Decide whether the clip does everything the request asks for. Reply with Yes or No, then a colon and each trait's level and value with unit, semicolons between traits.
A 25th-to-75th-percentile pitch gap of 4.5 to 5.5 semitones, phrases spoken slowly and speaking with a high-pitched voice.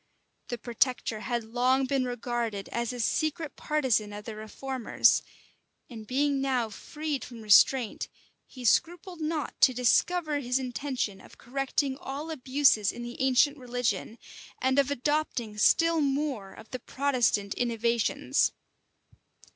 No: average, 3.3 semitones; slow, 130 wpm; very high, 255 Hz